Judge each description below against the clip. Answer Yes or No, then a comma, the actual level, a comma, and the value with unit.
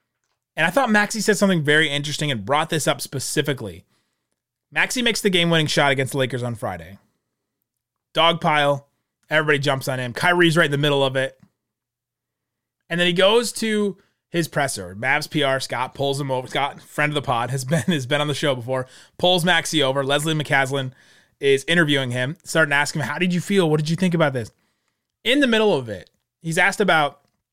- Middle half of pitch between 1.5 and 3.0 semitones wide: No, average, 4.4 semitones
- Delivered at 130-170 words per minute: No, average, 200 wpm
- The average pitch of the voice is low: No, medium, 145 Hz